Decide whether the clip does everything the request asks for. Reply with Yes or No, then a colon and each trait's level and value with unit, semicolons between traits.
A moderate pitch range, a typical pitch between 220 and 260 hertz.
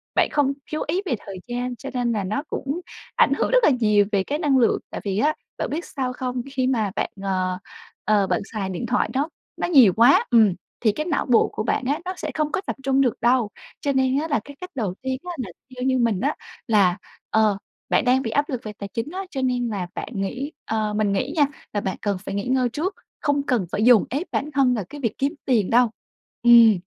Yes: average, 4.8 semitones; very high, 250 Hz